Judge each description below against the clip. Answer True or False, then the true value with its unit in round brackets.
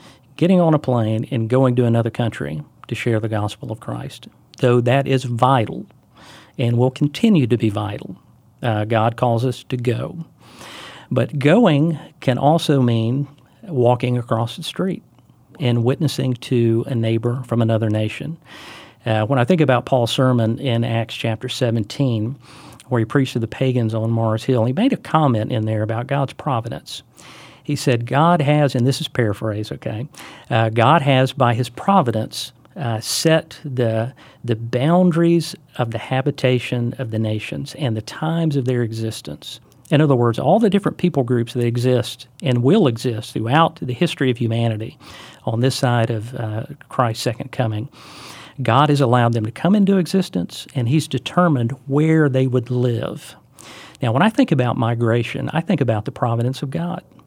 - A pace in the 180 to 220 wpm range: False (170 wpm)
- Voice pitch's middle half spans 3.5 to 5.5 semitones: True (3.8 semitones)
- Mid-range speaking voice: False (125 Hz)